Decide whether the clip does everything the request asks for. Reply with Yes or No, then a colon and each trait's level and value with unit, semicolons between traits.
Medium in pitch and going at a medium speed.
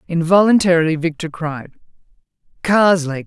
No: medium, 170 Hz; slow, 75 wpm